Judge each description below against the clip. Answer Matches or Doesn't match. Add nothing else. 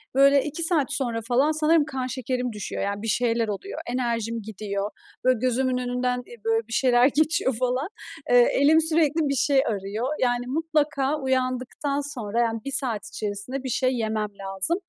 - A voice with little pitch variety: Doesn't match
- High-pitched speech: Matches